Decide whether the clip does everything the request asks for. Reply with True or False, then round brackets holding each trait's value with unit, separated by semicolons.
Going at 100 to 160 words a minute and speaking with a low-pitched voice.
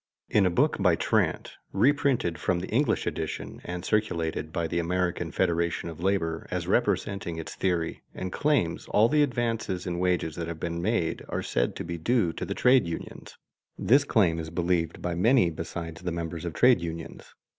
False (185 wpm; 85 Hz)